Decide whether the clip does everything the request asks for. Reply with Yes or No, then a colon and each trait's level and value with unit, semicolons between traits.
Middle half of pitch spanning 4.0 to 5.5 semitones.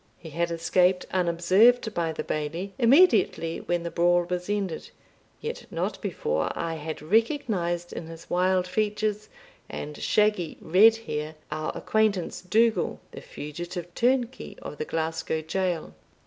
Yes: average, 4.4 semitones